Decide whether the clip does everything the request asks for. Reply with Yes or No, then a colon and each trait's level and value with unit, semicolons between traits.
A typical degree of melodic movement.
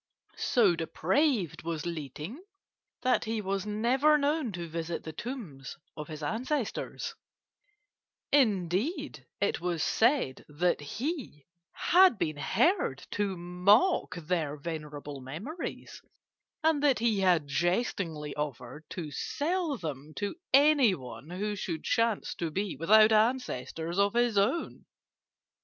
No: wide, 7.6 semitones